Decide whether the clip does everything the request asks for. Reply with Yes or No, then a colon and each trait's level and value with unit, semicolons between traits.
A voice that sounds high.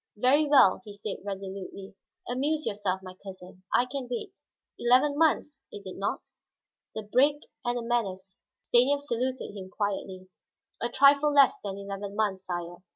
Yes: high, 215 Hz